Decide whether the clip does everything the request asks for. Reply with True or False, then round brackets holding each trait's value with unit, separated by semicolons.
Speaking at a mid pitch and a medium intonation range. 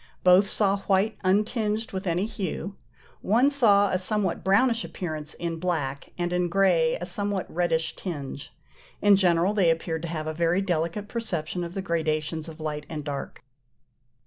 True (180 Hz; 3.7 semitones)